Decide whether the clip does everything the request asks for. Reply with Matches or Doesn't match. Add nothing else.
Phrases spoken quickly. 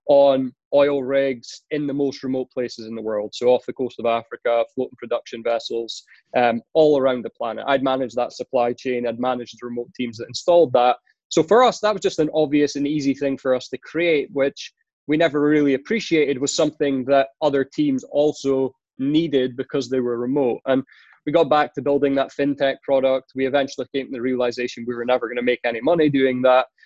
Matches